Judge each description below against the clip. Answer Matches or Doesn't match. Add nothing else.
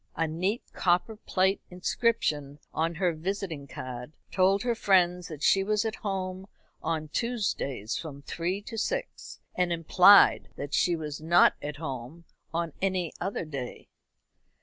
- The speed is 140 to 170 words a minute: Matches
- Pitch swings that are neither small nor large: Matches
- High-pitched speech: Doesn't match